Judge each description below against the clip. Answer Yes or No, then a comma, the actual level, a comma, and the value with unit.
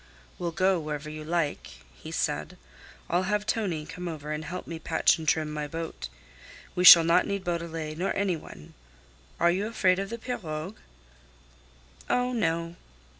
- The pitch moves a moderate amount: Yes, average, 3.6 semitones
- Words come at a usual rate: Yes, average, 165 wpm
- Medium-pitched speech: Yes, medium, 170 Hz